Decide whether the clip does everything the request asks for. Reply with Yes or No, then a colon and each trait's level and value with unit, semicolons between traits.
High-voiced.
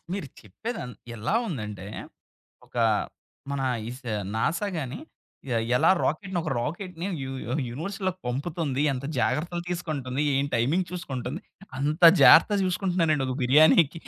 No: medium, 155 Hz